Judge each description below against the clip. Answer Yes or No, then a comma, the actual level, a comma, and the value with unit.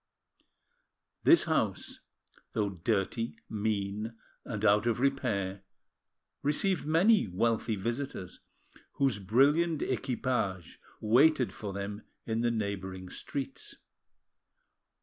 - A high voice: No, low, 110 Hz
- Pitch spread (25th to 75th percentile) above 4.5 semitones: Yes, average, 5.3 semitones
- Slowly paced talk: Yes, slow, 90 wpm